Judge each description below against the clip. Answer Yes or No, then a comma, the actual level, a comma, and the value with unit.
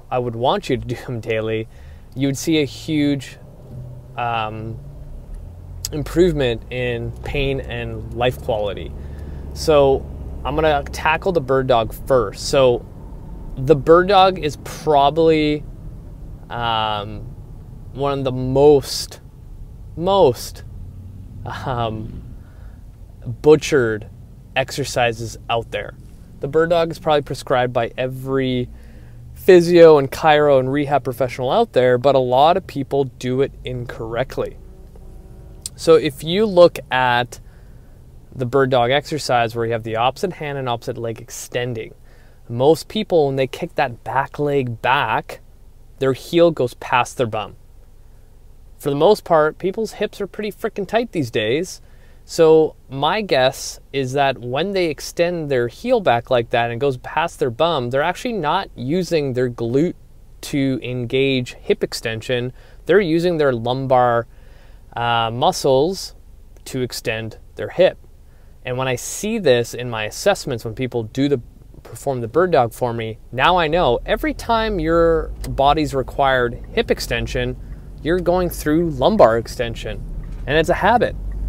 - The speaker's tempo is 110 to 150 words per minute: Yes, average, 140 wpm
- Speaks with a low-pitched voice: Yes, low, 130 Hz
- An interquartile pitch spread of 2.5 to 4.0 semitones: No, average, 4.7 semitones